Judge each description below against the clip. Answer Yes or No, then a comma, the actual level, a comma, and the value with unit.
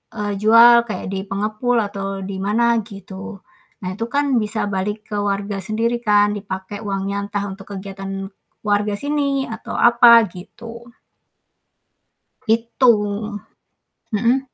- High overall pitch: Yes, high, 210 Hz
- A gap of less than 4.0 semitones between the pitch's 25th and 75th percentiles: Yes, average, 2.9 semitones